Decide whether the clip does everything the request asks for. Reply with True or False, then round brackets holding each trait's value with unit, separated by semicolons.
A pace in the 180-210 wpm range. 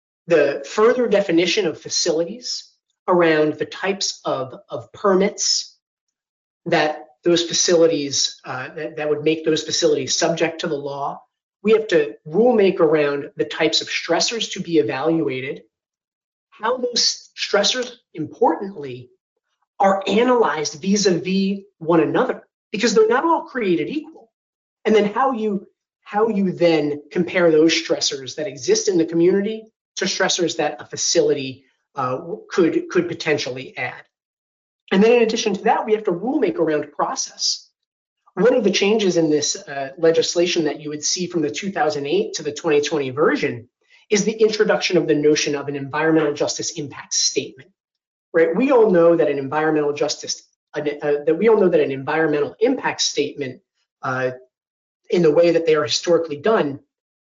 False (155 wpm)